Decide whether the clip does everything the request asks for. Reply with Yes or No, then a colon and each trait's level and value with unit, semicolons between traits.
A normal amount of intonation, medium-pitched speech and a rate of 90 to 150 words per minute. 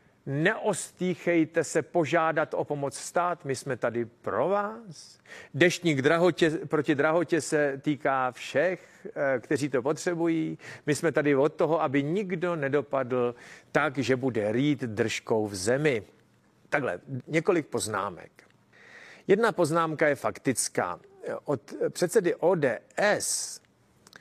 Yes: average, 4.2 semitones; medium, 155 Hz; slow, 115 wpm